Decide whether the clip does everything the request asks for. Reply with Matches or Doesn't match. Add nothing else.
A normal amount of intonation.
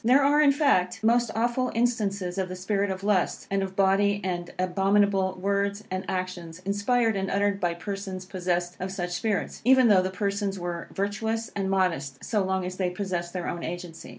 Doesn't match